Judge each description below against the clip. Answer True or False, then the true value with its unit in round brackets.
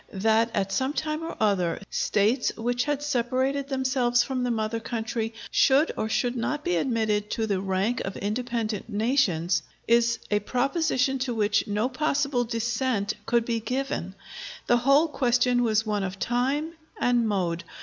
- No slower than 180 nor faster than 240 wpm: False (160 wpm)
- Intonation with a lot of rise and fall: False (3.6 semitones)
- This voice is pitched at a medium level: False (235 Hz)